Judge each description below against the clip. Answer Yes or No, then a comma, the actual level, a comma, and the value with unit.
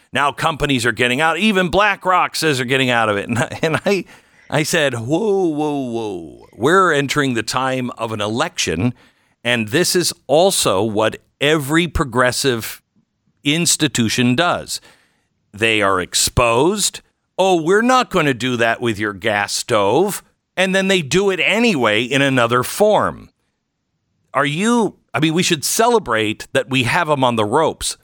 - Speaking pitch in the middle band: Yes, medium, 145 Hz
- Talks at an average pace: Yes, average, 160 wpm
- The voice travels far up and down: Yes, wide, 6.5 semitones